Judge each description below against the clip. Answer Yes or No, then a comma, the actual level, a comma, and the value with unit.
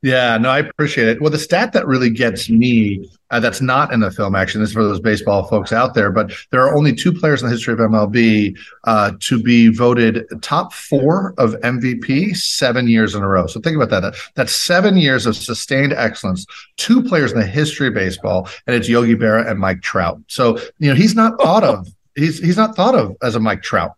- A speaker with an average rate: No, fast, 225 wpm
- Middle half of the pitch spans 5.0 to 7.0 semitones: Yes, average, 5.3 semitones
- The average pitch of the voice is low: Yes, low, 120 Hz